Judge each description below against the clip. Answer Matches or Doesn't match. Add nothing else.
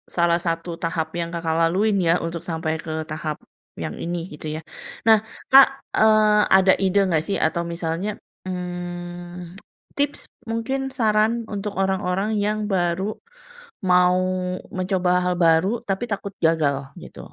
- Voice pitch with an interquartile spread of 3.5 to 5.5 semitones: Matches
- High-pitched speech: Doesn't match